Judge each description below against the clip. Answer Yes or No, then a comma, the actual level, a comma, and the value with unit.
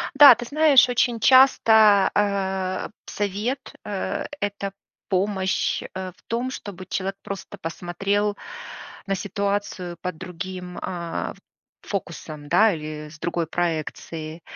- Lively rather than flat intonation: No, average, 2.9 semitones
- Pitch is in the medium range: No, high, 195 Hz